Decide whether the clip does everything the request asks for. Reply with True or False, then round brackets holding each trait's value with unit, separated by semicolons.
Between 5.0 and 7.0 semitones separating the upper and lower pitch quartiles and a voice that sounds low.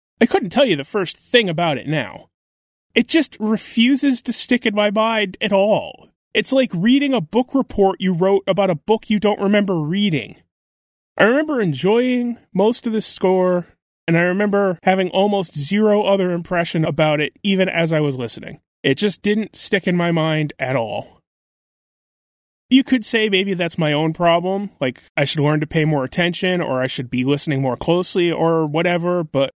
False (5.3 semitones; 185 Hz)